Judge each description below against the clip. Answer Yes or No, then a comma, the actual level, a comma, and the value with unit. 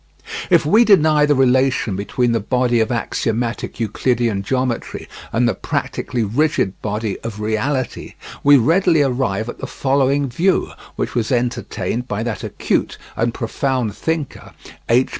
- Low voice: Yes, low, 125 Hz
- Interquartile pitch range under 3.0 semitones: No, average, 3.7 semitones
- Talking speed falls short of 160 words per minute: Yes, average, 140 wpm